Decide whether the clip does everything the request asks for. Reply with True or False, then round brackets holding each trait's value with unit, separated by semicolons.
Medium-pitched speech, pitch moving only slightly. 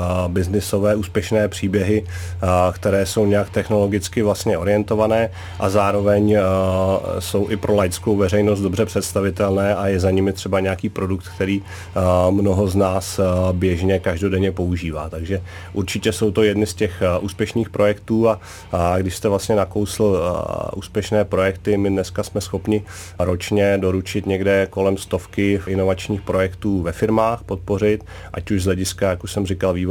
False (100 Hz; 1.9 semitones)